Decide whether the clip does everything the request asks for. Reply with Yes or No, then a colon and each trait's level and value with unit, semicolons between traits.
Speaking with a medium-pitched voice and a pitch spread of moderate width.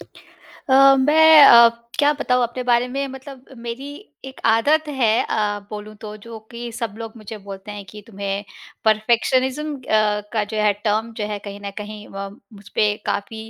No: high, 230 Hz; average, 3.9 semitones